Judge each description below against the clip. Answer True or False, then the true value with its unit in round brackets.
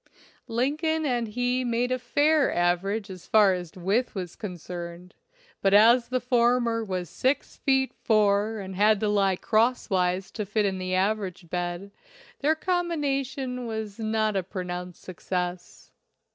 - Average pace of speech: True (145 wpm)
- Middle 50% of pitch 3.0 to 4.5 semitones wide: False (5.0 semitones)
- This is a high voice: True (215 Hz)